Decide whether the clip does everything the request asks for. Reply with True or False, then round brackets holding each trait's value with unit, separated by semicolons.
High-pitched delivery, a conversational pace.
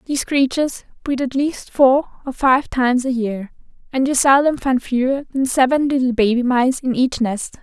True (260 Hz; 190 wpm)